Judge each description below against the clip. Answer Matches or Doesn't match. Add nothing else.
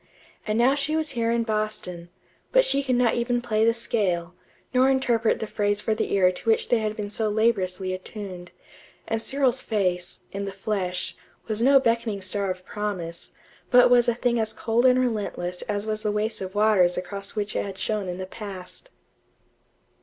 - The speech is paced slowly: Doesn't match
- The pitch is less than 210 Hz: Doesn't match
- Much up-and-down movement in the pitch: Doesn't match